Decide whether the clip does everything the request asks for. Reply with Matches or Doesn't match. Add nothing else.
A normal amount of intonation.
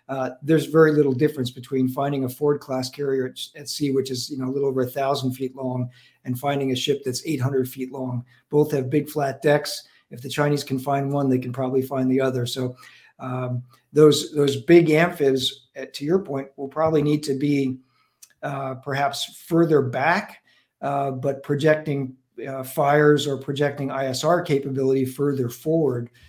Doesn't match